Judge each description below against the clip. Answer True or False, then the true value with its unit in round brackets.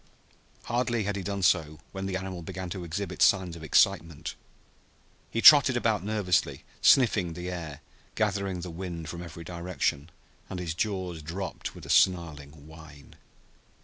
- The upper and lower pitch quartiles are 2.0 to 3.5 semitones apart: True (3.1 semitones)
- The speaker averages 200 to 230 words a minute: False (150 wpm)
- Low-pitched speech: True (90 Hz)